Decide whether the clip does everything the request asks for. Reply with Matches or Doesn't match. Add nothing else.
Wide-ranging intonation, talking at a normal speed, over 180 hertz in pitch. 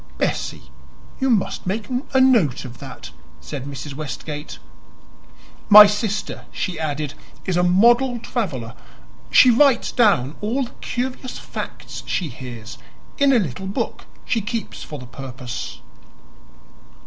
Doesn't match